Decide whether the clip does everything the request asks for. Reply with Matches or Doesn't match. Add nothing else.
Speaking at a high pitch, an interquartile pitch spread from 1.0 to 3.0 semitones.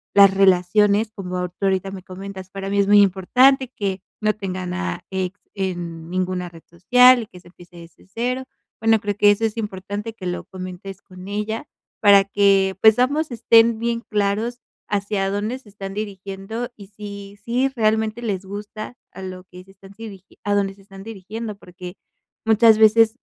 Matches